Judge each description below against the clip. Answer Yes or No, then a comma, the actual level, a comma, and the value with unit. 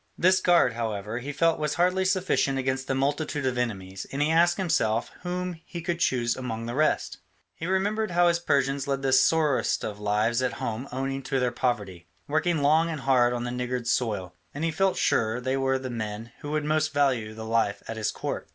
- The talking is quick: Yes, fast, 210 wpm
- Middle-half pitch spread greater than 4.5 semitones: Yes, average, 5.2 semitones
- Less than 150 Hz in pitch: Yes, low, 135 Hz